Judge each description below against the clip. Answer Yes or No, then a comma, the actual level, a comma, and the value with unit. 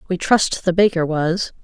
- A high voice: No, medium, 175 Hz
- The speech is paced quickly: No, average, 185 wpm